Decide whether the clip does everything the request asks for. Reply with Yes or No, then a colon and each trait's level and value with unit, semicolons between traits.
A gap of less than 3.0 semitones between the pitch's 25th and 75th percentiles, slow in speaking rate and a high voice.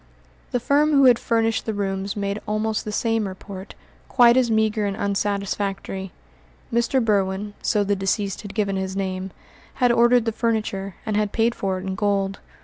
No: narrow, 2.6 semitones; average, 175 wpm; high, 205 Hz